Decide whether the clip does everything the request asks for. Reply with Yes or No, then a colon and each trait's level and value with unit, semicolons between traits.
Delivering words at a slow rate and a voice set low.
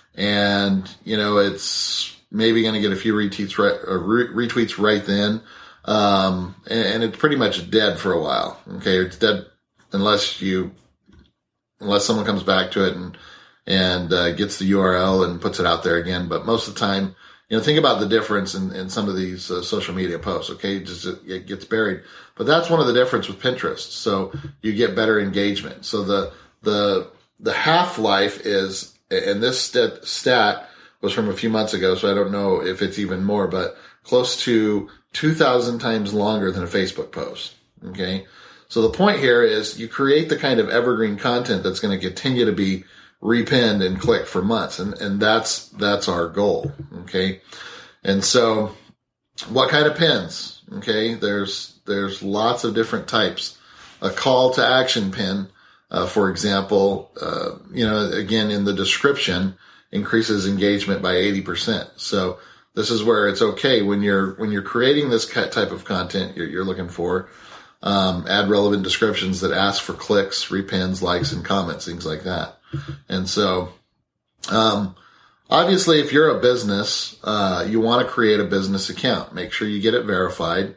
No: average, 180 wpm; low, 100 Hz